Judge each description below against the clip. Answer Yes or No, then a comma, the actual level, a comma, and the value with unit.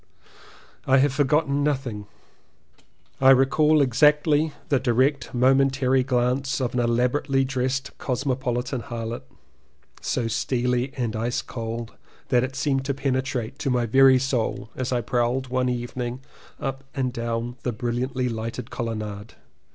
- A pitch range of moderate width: No, narrow, 2.0 semitones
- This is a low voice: Yes, low, 130 Hz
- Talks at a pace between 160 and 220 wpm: No, slow, 135 wpm